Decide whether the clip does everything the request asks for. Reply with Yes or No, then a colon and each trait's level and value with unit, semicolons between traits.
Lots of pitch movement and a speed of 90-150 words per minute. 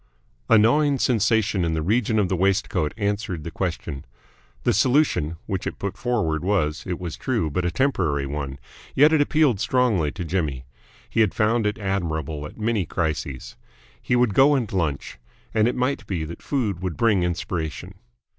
No: wide, 5.9 semitones; average, 175 wpm